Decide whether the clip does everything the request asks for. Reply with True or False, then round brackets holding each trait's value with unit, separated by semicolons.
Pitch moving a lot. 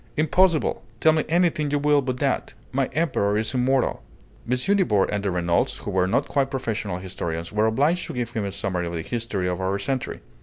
True (7.0 semitones)